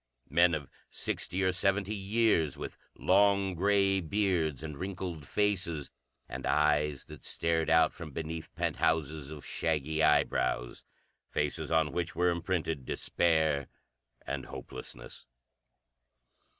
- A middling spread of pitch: Yes, average, 3.9 semitones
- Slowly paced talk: Yes, slow, 115 wpm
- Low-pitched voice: Yes, very low, 80 Hz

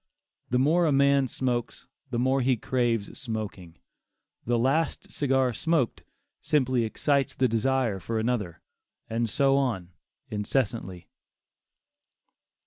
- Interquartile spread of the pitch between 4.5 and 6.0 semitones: No, average, 3.3 semitones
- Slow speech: Yes, slow, 115 wpm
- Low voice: Yes, low, 125 Hz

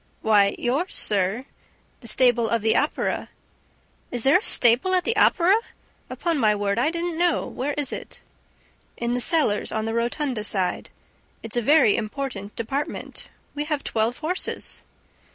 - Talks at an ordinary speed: Yes, average, 155 wpm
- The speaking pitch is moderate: No, high, 245 Hz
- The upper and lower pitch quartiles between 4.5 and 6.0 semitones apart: Yes, wide, 5.6 semitones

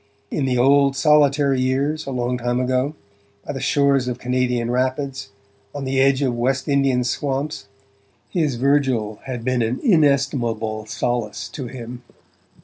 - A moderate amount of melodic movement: No, narrow, 2.2 semitones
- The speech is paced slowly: No, average, 145 wpm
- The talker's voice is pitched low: Yes, low, 130 Hz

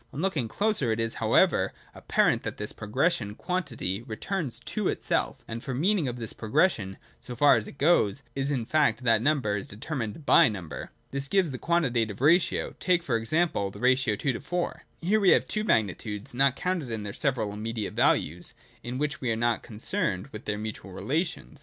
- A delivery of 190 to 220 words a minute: Yes, average, 200 wpm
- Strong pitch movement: Yes, wide, 6.2 semitones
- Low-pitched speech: Yes, low, 125 Hz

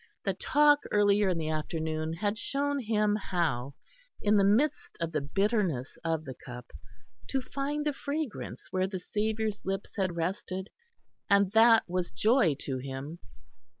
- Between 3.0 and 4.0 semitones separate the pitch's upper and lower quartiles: No, wide, 5.5 semitones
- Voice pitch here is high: Yes, high, 195 Hz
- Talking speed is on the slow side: No, average, 150 wpm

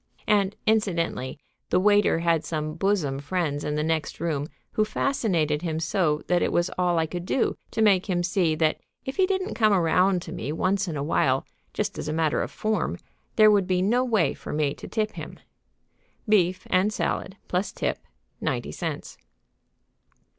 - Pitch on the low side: No, medium, 180 Hz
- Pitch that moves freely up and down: No, average, 4.6 semitones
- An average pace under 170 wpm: No, average, 180 wpm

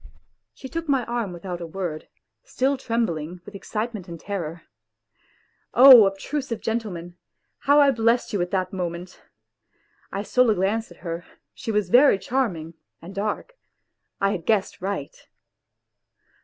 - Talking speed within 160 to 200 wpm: No, average, 145 wpm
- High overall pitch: Yes, high, 200 Hz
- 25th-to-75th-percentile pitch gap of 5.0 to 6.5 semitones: Yes, average, 5.3 semitones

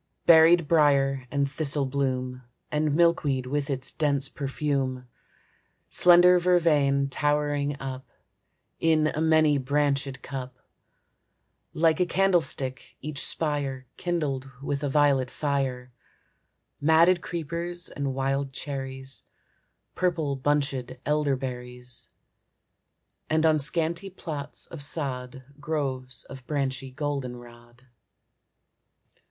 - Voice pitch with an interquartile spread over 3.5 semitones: No, average, 2.9 semitones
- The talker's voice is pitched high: No, medium, 140 Hz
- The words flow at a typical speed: No, slow, 100 wpm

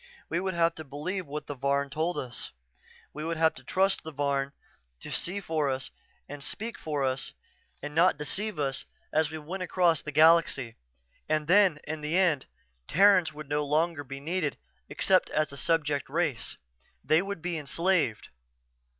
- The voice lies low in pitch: No, medium, 155 Hz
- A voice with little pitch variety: No, average, 3.4 semitones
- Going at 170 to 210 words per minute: Yes, average, 175 wpm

